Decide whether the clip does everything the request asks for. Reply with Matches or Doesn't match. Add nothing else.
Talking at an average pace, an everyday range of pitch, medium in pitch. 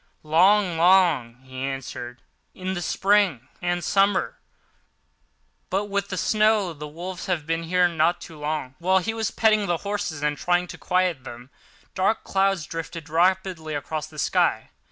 Matches